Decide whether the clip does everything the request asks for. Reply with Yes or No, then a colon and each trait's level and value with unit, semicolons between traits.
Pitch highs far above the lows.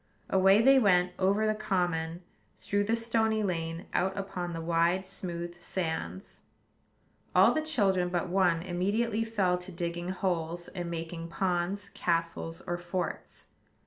No: narrow, 2.6 semitones